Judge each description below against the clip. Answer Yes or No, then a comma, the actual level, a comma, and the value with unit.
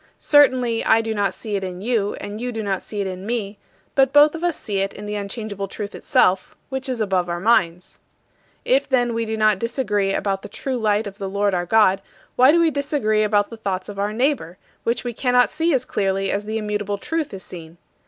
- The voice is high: Yes, high, 215 Hz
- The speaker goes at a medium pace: No, fast, 230 wpm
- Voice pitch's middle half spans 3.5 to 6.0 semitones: Yes, average, 3.8 semitones